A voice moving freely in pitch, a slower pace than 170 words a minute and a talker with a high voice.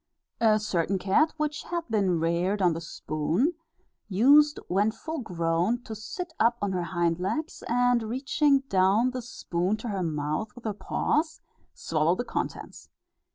Yes: wide, 6.0 semitones; average, 155 wpm; high, 210 Hz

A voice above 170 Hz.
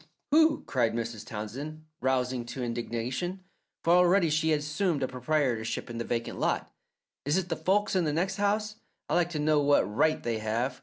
No: medium, 145 Hz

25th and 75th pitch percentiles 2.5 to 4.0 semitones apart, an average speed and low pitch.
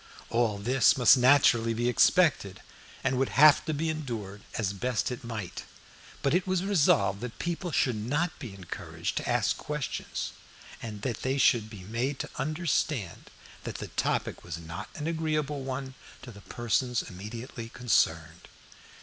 No: wide, 5.4 semitones; average, 160 wpm; low, 125 Hz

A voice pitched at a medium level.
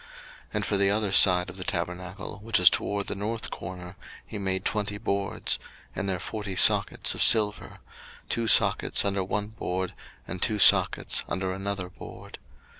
No: low, 100 Hz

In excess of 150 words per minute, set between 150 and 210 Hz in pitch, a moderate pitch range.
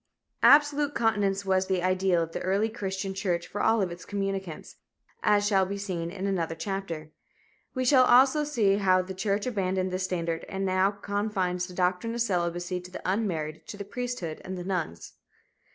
No: average, 185 wpm; high, 190 Hz; narrow, 2.3 semitones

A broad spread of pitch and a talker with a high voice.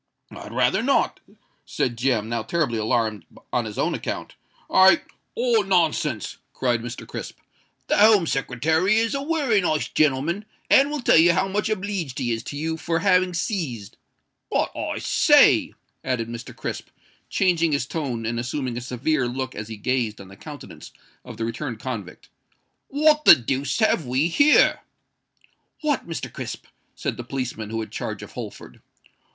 No: wide, 7.9 semitones; medium, 140 Hz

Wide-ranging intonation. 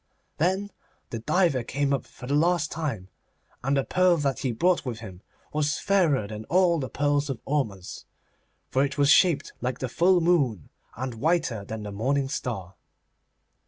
Yes: wide, 5.9 semitones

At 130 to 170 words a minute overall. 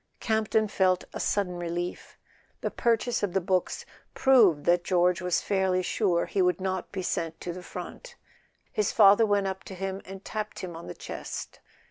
No: average, 180 wpm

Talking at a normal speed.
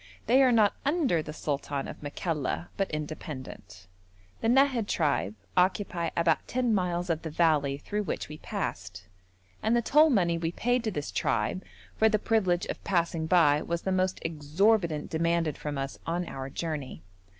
Yes: average, 170 wpm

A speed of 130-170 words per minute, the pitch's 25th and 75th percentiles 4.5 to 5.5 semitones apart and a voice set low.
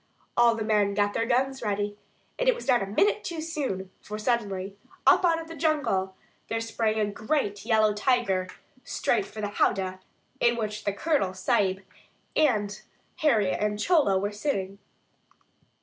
No: average, 165 wpm; average, 5.0 semitones; high, 215 Hz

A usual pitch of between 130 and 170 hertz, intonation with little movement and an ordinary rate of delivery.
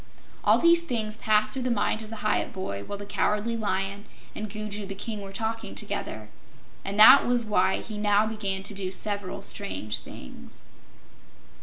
No: high, 210 Hz; narrow, 2.0 semitones; average, 175 wpm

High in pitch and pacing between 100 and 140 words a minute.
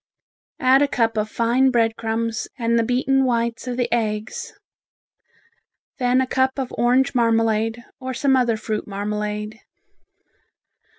Yes: high, 235 Hz; slow, 135 wpm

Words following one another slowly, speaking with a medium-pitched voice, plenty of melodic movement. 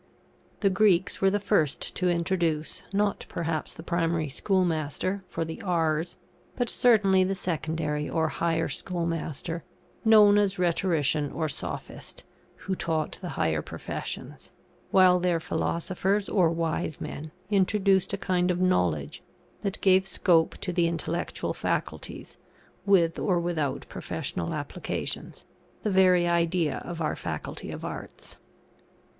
No: slow, 130 wpm; medium, 175 Hz; average, 2.9 semitones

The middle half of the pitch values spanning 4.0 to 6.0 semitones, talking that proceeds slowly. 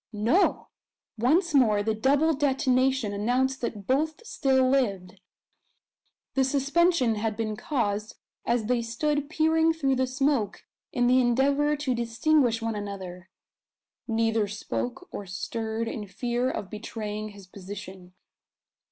Yes: average, 4.4 semitones; slow, 125 wpm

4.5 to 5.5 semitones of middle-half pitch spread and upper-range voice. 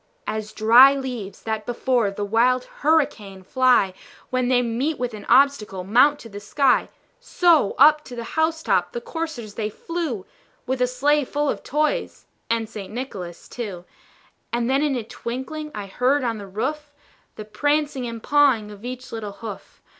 Yes: average, 5.0 semitones; high, 245 Hz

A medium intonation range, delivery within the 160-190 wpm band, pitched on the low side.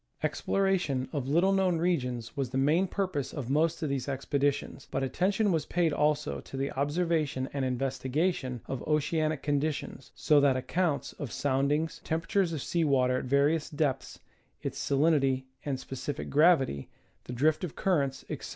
No: average, 3.5 semitones; average, 165 wpm; medium, 145 Hz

